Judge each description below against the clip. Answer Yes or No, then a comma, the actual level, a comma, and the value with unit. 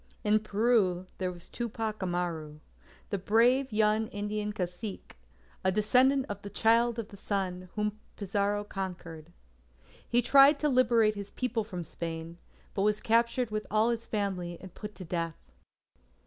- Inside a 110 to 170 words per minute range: Yes, average, 150 wpm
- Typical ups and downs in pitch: Yes, average, 3.6 semitones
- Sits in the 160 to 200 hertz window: No, high, 210 Hz